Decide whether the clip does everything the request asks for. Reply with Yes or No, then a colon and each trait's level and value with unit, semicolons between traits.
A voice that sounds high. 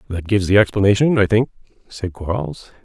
No: low, 100 Hz